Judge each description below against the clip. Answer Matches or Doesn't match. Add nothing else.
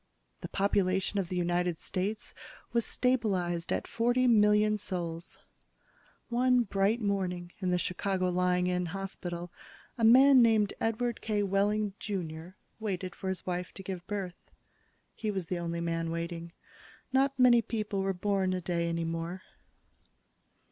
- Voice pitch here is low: Doesn't match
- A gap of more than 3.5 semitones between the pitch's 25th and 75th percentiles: Doesn't match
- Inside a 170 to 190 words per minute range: Doesn't match